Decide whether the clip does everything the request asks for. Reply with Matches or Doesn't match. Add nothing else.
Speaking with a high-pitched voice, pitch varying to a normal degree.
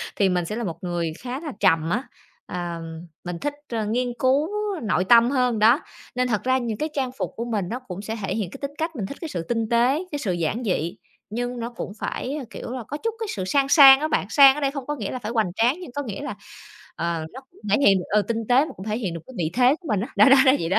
Doesn't match